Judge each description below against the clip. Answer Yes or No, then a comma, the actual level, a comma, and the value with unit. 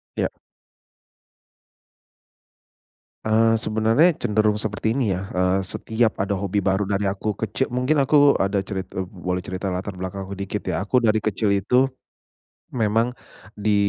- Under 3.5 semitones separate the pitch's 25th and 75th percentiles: Yes, narrow, 2.5 semitones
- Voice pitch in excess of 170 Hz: No, low, 105 Hz